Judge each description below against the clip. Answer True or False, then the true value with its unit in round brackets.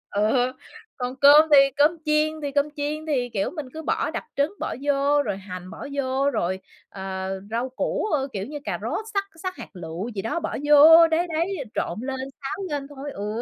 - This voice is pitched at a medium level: False (280 Hz)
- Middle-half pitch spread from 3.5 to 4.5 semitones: False (5.3 semitones)